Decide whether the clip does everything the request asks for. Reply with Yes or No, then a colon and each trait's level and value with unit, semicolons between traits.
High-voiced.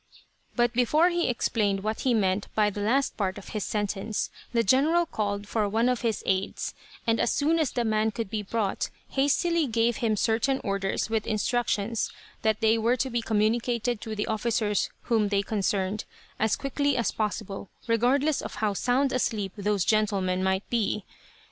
Yes: high, 220 Hz